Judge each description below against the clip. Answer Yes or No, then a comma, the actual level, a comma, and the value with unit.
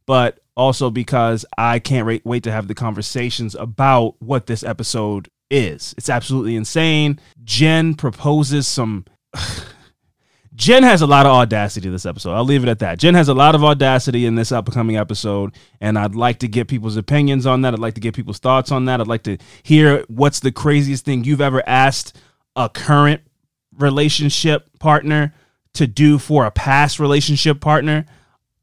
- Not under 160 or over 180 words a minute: Yes, average, 175 wpm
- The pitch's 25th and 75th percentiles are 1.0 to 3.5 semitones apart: No, average, 4.1 semitones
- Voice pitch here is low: Yes, low, 130 Hz